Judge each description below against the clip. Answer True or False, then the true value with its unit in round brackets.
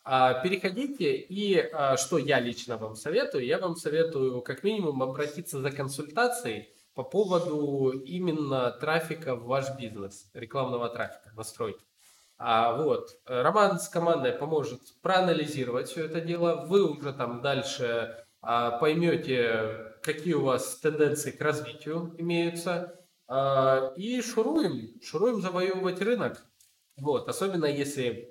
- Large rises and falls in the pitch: True (5.8 semitones)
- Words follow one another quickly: False (115 wpm)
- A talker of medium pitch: True (150 Hz)